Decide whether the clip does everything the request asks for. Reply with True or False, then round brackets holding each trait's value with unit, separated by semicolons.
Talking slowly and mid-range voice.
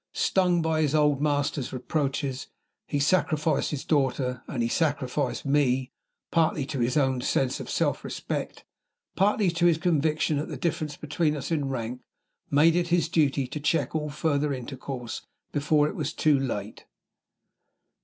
False (155 wpm; 145 Hz)